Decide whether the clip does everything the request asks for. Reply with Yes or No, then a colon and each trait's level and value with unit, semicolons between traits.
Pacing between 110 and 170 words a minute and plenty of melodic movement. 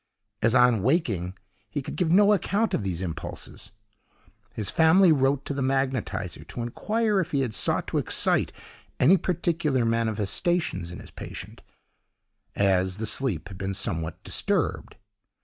Yes: average, 150 wpm; wide, 8.8 semitones